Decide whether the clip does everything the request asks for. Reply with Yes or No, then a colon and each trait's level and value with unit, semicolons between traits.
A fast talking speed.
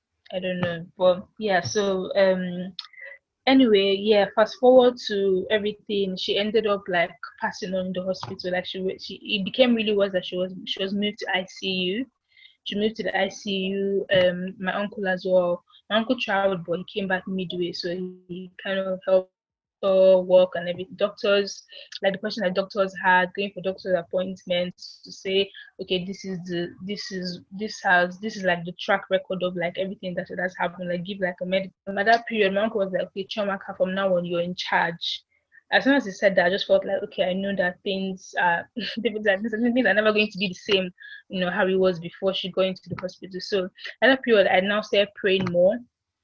Yes: fast, 215 wpm